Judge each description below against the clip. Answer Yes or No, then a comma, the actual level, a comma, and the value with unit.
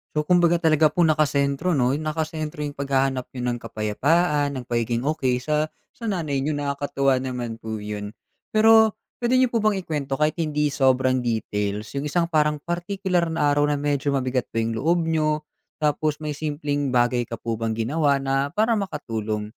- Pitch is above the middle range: No, medium, 145 Hz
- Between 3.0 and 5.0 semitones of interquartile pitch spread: Yes, average, 3.7 semitones